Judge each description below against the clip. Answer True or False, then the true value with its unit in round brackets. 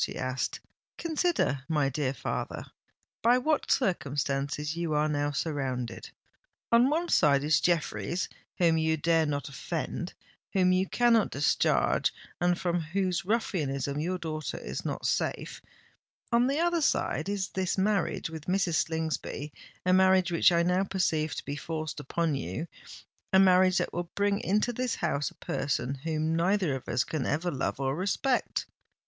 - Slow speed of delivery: False (150 wpm)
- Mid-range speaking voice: True (170 Hz)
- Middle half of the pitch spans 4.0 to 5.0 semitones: True (4.4 semitones)